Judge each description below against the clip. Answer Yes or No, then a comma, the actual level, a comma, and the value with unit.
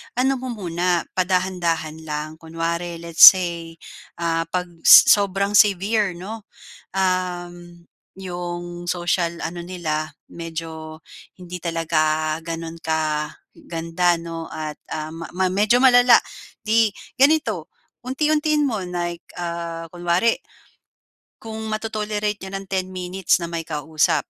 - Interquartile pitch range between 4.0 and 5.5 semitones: No, average, 2.9 semitones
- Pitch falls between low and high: Yes, medium, 175 Hz